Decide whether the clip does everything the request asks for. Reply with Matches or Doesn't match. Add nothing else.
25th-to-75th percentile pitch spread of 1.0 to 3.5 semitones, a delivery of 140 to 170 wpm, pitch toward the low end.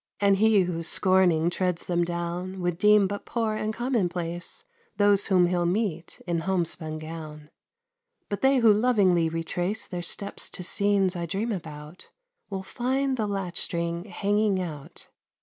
Doesn't match